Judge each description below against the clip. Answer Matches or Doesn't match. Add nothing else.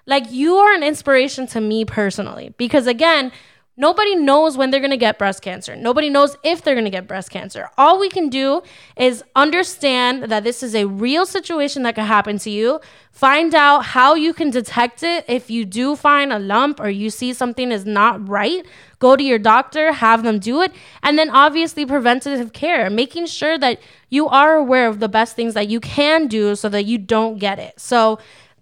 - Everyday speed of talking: Doesn't match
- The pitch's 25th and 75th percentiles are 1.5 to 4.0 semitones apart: Doesn't match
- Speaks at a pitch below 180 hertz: Doesn't match